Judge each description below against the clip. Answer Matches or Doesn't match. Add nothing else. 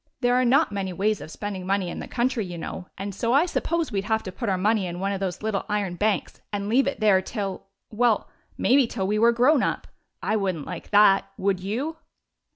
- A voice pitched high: Matches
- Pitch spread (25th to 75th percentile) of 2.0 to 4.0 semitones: Matches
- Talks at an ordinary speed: Doesn't match